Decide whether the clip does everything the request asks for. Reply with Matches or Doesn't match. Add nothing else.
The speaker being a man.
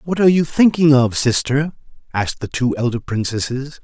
Matches